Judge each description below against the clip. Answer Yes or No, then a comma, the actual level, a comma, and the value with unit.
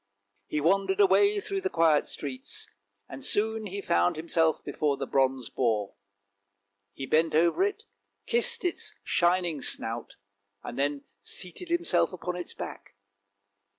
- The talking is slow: Yes, slow, 130 wpm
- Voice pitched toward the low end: No, medium, 170 Hz